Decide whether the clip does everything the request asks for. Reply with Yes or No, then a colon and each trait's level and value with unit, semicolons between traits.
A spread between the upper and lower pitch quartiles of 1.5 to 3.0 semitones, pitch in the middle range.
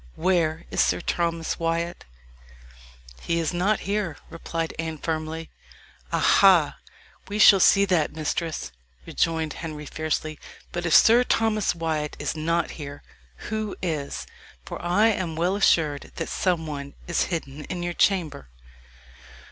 Yes: narrow, 2.5 semitones; medium, 165 Hz